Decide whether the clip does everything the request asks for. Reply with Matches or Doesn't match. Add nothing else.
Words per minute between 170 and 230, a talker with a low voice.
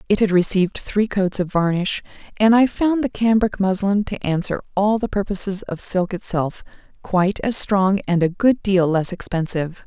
Doesn't match